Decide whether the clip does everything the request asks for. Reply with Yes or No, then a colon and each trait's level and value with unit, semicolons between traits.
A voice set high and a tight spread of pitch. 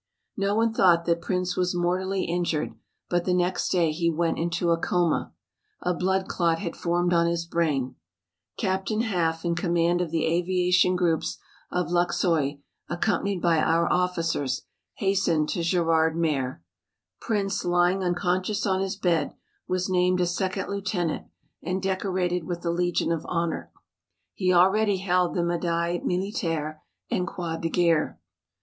No: medium, 175 Hz; narrow, 1.8 semitones